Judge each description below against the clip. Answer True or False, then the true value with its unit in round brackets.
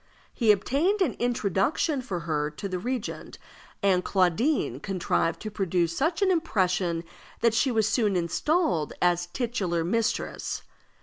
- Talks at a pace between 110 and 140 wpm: True (135 wpm)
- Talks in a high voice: True (200 Hz)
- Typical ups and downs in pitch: False (6.4 semitones)